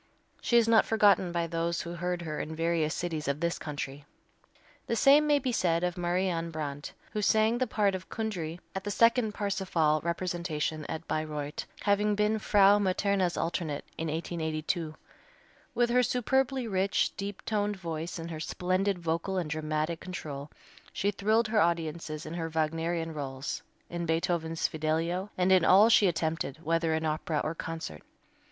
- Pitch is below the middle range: No, medium, 170 Hz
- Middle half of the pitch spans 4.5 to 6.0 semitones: No, average, 4.1 semitones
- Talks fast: No, average, 165 wpm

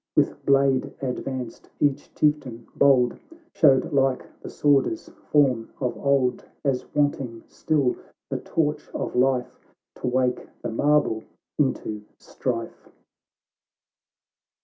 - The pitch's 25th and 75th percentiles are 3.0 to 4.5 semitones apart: No, narrow, 2.4 semitones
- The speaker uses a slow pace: Yes, slow, 105 wpm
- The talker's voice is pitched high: No, low, 135 Hz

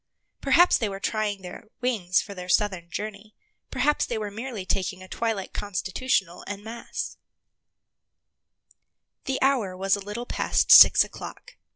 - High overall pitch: Yes, high, 205 Hz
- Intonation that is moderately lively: Yes, average, 3.4 semitones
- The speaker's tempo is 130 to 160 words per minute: Yes, average, 145 wpm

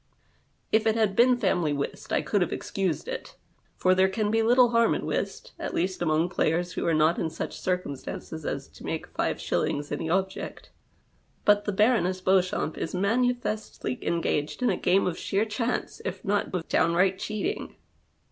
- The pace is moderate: Yes, average, 175 wpm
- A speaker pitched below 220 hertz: Yes, high, 190 Hz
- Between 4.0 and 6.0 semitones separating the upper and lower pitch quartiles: Yes, average, 4.3 semitones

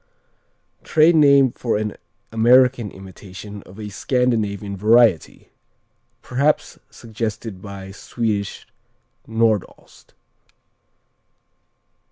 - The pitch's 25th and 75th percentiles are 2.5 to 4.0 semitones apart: Yes, average, 3.5 semitones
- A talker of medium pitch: No, low, 110 Hz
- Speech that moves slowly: Yes, slow, 80 wpm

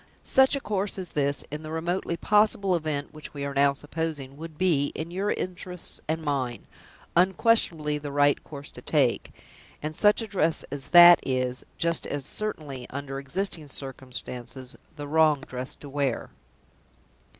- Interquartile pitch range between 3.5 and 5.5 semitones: Yes, average, 3.9 semitones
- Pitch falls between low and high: Yes, medium, 150 Hz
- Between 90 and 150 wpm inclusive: No, average, 160 wpm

